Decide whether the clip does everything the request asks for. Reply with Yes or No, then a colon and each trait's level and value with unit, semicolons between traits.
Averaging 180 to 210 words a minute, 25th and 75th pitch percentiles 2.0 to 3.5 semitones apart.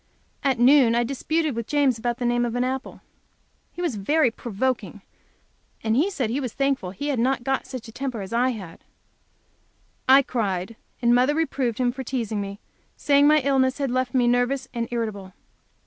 Yes: average, 185 wpm; average, 2.9 semitones